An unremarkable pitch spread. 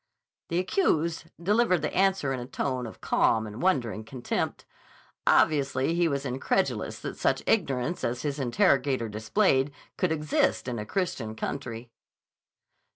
No: wide, 5.8 semitones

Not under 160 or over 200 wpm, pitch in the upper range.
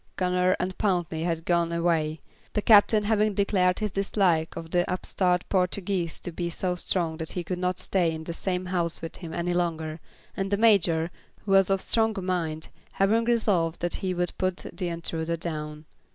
No: average, 185 wpm; medium, 180 Hz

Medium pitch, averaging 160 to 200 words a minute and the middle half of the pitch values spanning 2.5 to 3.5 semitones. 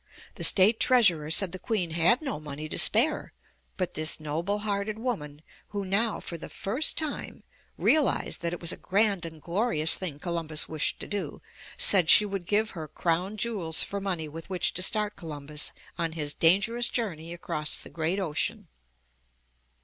No: medium, 180 Hz; average, 170 wpm; average, 4.7 semitones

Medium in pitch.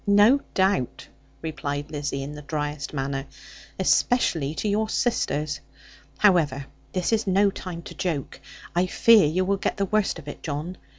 Yes: medium, 165 Hz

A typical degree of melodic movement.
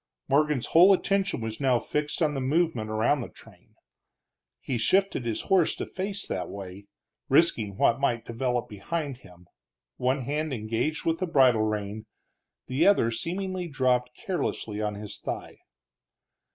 No: wide, 6.4 semitones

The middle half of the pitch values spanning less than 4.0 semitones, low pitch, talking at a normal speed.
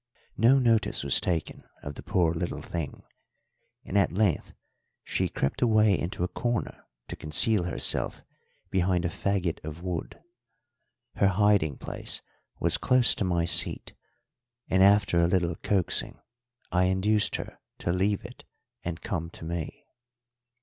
Yes: average, 3.3 semitones; very low, 90 Hz; average, 145 wpm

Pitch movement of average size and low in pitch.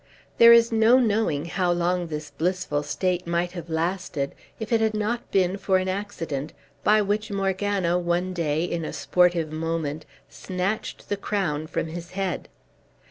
No: average, 3.6 semitones; medium, 180 Hz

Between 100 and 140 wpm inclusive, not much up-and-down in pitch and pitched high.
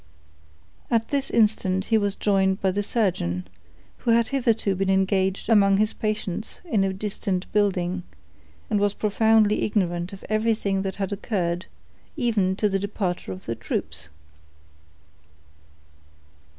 Yes: slow, 135 wpm; narrow, 2.3 semitones; high, 200 Hz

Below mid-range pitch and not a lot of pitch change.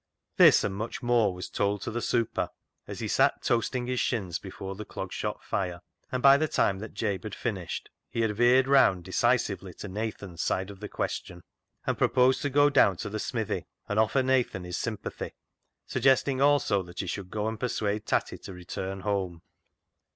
No: low, 105 Hz; average, 4.3 semitones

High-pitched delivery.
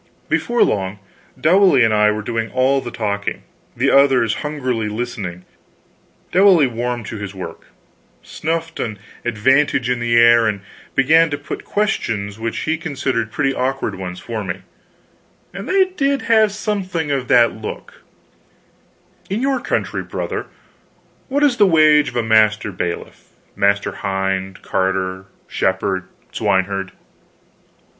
No: low, 120 Hz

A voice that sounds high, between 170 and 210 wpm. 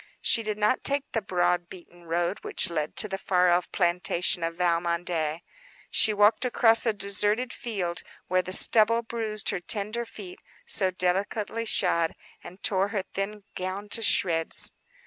No: high, 195 Hz; average, 160 wpm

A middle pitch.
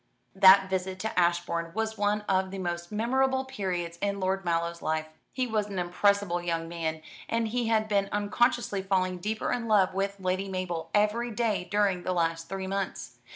No: high, 195 Hz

